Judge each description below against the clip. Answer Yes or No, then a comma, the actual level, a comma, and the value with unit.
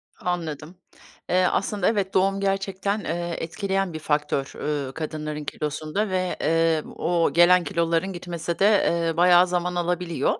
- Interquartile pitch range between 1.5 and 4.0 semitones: Yes, average, 2.7 semitones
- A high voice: No, medium, 175 Hz